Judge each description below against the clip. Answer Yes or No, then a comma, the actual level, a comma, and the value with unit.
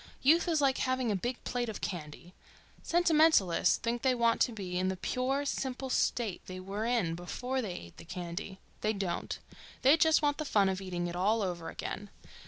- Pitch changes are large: Yes, wide, 6.0 semitones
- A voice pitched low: No, high, 220 Hz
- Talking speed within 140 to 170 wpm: No, average, 195 wpm